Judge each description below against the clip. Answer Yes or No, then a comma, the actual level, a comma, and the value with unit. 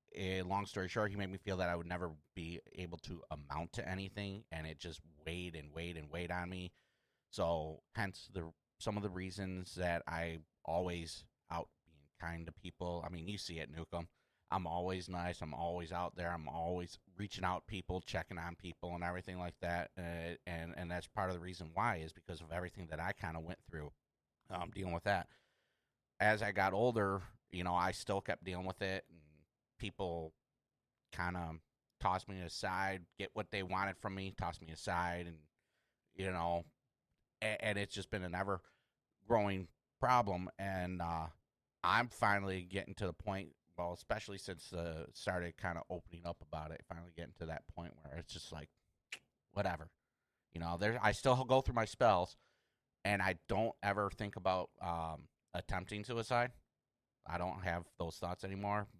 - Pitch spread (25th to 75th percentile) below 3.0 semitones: Yes, narrow, 2.6 semitones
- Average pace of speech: Yes, average, 190 wpm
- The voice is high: No, very low, 90 Hz